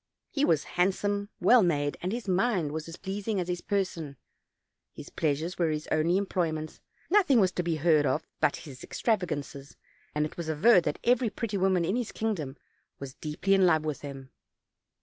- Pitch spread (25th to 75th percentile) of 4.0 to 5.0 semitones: Yes, average, 4.7 semitones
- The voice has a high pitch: No, medium, 175 Hz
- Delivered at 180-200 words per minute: Yes, average, 195 wpm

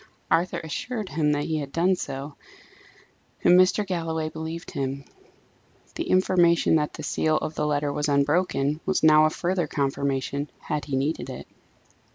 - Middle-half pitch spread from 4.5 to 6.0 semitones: No, average, 3.1 semitones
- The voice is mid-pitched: Yes, medium, 155 Hz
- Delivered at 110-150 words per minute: No, average, 160 wpm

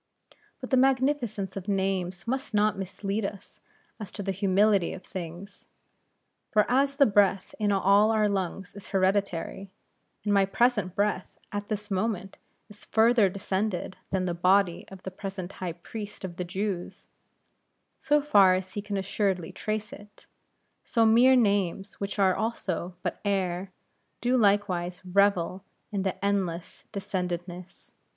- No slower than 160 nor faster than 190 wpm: No, average, 145 wpm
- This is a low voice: No, high, 195 Hz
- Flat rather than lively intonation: Yes, narrow, 2.2 semitones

